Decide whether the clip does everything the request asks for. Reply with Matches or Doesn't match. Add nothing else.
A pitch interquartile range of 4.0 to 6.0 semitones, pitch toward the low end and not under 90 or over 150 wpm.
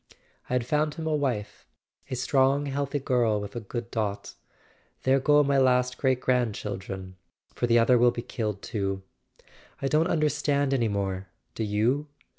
Doesn't match